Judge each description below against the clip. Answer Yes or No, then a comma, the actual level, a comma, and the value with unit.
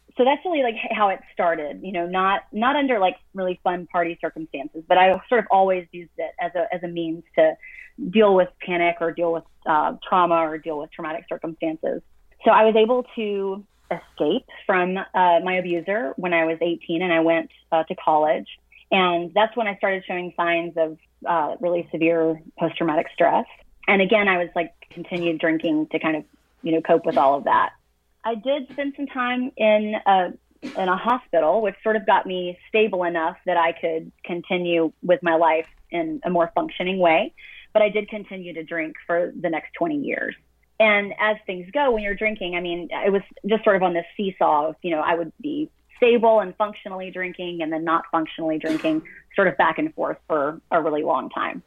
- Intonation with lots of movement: No, average, 4.3 semitones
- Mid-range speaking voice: Yes, medium, 180 Hz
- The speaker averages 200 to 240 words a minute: Yes, fast, 205 wpm